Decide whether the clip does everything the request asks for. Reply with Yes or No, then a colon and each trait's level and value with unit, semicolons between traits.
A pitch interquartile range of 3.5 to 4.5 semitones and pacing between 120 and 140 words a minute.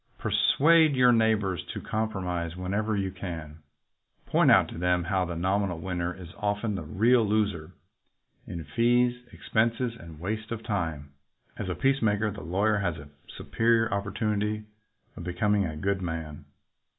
No: average, 4.1 semitones; average, 150 wpm